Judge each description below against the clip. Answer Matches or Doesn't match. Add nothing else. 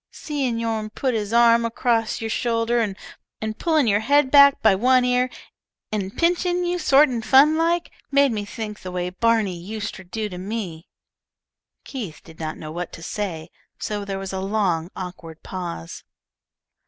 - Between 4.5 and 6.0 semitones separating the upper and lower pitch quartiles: Matches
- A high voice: Matches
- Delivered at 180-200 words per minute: Doesn't match